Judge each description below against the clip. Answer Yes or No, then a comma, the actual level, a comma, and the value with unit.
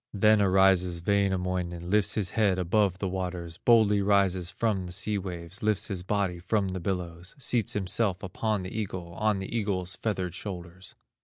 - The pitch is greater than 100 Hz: No, very low, 95 Hz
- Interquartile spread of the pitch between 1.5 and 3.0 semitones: Yes, narrow, 2.4 semitones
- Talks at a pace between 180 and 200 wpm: No, average, 165 wpm